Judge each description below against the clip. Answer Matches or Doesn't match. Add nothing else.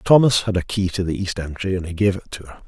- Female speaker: Doesn't match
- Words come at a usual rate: Doesn't match